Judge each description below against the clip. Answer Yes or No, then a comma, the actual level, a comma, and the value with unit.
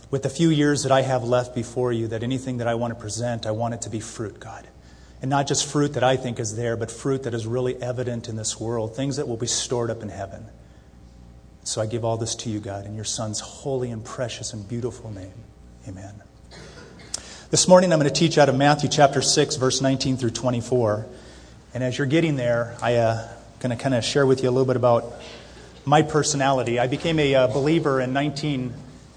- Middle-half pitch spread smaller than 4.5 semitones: Yes, average, 3.2 semitones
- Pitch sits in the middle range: No, low, 120 Hz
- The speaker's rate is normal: No, fast, 230 wpm